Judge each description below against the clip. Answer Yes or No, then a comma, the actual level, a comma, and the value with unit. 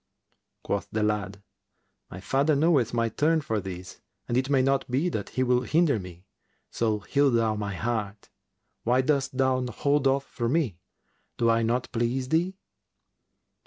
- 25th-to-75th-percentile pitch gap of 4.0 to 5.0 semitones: Yes, average, 4.3 semitones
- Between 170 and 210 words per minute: No, average, 160 wpm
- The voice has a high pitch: No, low, 125 Hz